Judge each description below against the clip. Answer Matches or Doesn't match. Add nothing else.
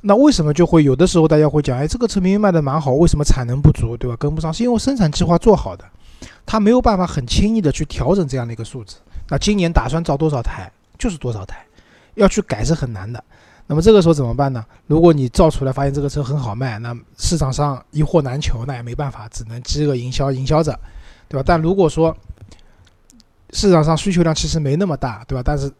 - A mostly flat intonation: Doesn't match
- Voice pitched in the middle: Matches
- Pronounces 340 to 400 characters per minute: Matches